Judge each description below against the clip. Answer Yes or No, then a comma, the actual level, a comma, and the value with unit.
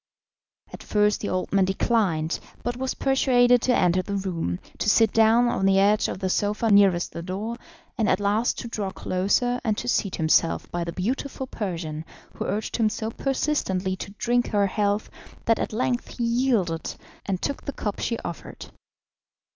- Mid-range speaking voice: No, high, 210 Hz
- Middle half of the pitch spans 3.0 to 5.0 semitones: Yes, average, 4.2 semitones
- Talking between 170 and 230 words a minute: Yes, average, 180 wpm